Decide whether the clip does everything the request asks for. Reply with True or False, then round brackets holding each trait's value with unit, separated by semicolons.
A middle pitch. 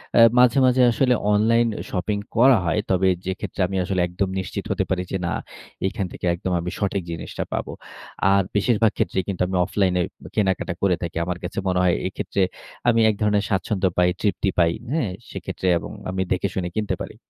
False (95 Hz)